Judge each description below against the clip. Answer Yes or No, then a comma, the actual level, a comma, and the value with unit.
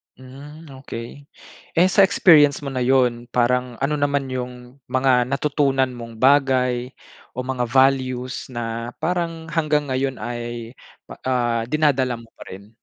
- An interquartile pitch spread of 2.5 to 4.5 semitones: Yes, average, 2.8 semitones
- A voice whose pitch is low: Yes, low, 130 Hz